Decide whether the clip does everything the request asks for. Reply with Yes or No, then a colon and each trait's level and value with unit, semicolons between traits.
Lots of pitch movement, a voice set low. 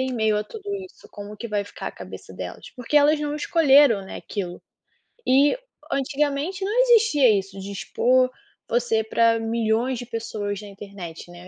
No: wide, 5.9 semitones; high, 235 Hz